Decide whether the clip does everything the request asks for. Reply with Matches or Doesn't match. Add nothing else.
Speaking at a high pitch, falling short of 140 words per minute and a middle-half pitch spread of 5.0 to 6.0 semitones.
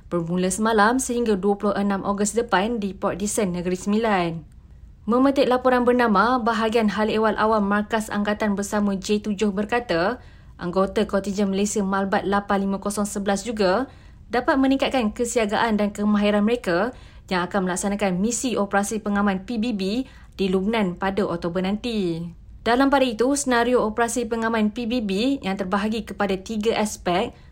Doesn't match